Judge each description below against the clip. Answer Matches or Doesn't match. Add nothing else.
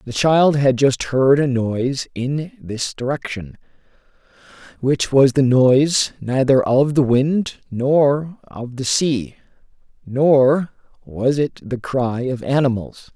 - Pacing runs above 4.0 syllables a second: Doesn't match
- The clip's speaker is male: Matches